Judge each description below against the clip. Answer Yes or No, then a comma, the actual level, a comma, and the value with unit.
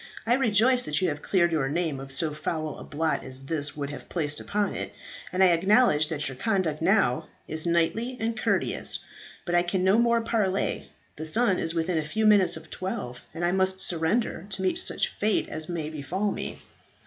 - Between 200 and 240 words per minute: Yes, fast, 205 wpm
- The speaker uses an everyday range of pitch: Yes, average, 4.6 semitones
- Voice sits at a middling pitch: Yes, medium, 175 Hz